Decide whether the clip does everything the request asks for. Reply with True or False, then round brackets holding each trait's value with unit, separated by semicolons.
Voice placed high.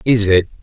False (105 Hz)